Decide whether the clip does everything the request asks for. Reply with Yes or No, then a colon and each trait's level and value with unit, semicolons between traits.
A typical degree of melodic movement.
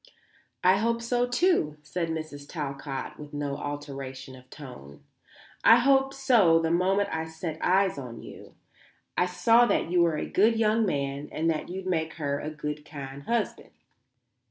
No: wide, 5.9 semitones